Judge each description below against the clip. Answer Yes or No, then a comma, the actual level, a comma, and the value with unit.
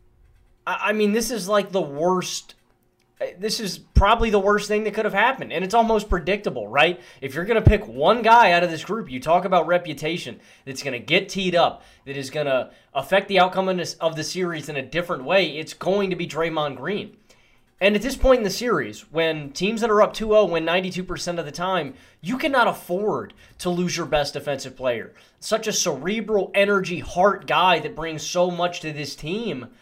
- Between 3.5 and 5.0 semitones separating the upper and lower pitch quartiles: Yes, average, 4.5 semitones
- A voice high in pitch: No, medium, 180 Hz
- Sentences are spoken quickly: Yes, fast, 215 wpm